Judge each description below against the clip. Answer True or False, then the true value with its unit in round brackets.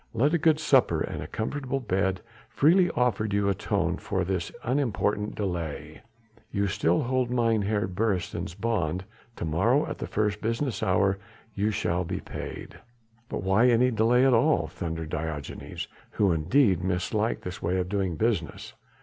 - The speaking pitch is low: True (105 Hz)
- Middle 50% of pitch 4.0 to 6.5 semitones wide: True (4.9 semitones)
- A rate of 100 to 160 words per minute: True (155 wpm)